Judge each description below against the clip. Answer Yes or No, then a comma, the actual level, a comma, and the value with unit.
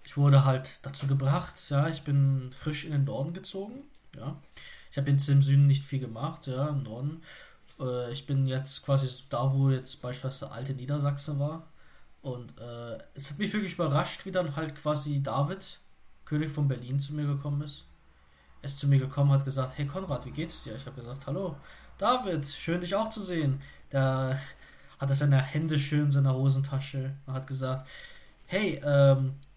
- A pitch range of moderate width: No, narrow, 2.0 semitones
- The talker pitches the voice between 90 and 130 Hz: No, medium, 140 Hz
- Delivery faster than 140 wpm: Yes, average, 185 wpm